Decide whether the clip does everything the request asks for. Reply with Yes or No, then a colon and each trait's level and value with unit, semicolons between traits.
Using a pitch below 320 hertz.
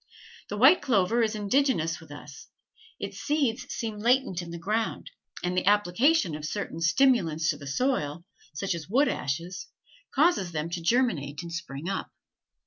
Yes: medium, 185 Hz